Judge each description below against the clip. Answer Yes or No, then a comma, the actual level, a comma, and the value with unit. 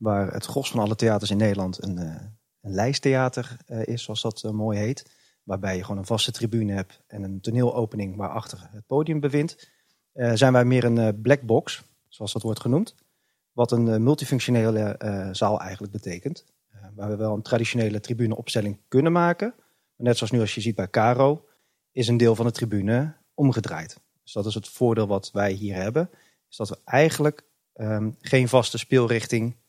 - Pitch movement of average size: Yes, average, 3.2 semitones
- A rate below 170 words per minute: No, average, 180 wpm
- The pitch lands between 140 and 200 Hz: No, low, 115 Hz